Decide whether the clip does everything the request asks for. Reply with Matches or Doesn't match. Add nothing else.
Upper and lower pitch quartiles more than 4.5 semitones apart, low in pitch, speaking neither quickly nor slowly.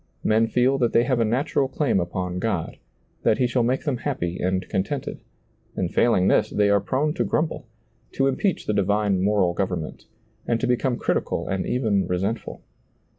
Matches